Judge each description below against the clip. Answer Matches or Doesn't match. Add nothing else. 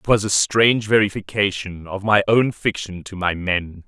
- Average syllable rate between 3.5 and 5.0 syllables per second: Matches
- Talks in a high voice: Doesn't match